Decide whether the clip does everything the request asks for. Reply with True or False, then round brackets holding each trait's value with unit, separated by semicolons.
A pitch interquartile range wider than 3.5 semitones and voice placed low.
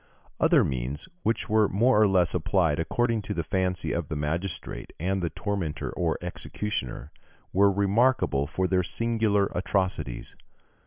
True (4.2 semitones; 95 Hz)